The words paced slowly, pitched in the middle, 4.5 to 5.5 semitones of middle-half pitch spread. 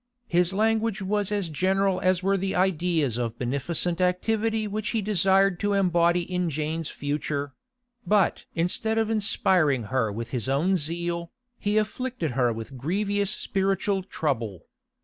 No: average, 145 wpm; medium, 180 Hz; average, 5.0 semitones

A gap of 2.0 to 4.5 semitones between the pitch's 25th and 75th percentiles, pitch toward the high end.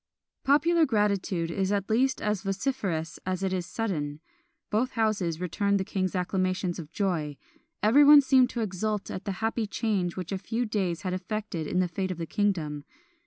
Yes: average, 3.3 semitones; high, 195 Hz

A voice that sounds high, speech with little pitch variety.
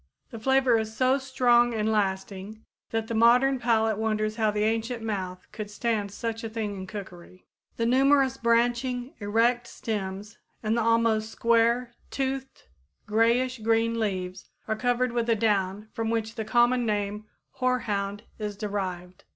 Yes: high, 225 Hz; narrow, 2.3 semitones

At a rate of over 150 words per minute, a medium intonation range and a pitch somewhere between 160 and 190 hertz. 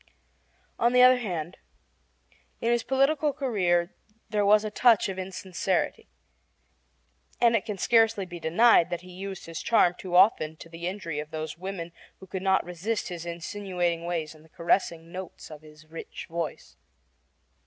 Yes: average, 165 wpm; average, 4.0 semitones; medium, 185 Hz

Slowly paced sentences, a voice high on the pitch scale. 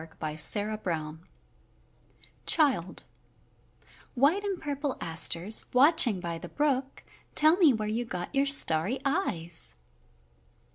Yes: slow, 105 wpm; high, 240 Hz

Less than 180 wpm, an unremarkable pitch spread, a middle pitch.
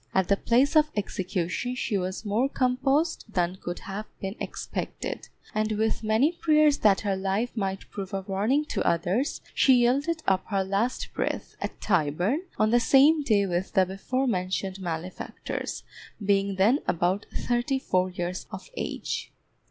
No: average, 160 wpm; average, 5.0 semitones; high, 205 Hz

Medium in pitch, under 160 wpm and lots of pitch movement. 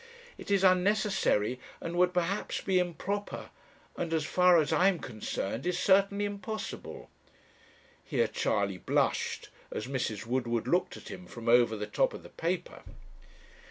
Yes: medium, 175 Hz; average, 150 wpm; wide, 8.0 semitones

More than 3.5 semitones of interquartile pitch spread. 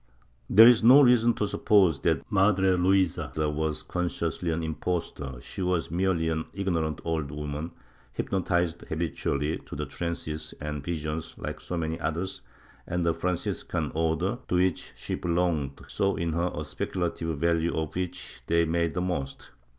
No: narrow, 2.6 semitones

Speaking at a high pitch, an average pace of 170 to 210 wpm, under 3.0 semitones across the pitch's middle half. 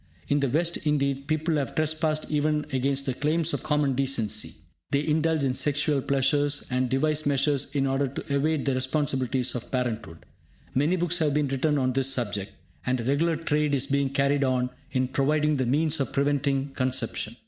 No: medium, 140 Hz; average, 180 wpm; narrow, 2.4 semitones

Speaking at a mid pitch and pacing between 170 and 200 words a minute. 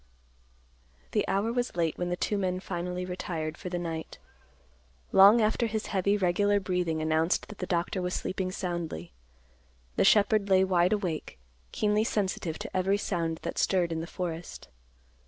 No: medium, 180 Hz; average, 160 wpm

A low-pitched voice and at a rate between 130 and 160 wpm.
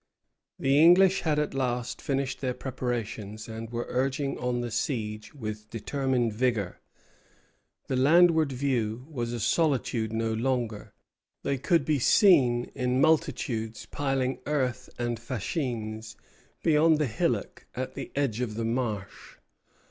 Yes: low, 125 Hz; slow, 135 wpm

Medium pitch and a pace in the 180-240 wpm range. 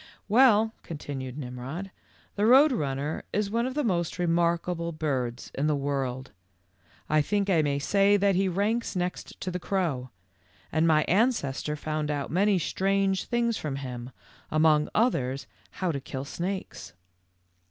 No: medium, 170 Hz; average, 155 wpm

